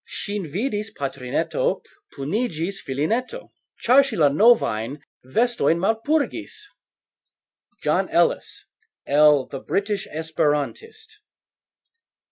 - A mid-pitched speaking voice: No, high, 195 Hz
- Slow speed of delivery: Yes, slow, 85 wpm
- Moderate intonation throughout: No, wide, 8.8 semitones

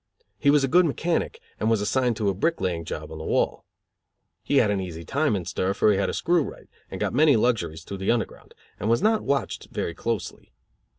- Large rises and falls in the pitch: Yes, wide, 7.1 semitones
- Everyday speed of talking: No, fast, 230 wpm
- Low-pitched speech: Yes, low, 110 Hz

